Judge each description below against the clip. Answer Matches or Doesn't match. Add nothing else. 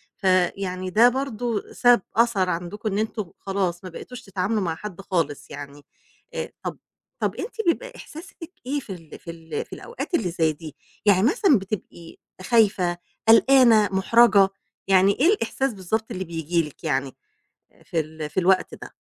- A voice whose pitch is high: Matches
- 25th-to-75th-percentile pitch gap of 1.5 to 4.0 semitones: Doesn't match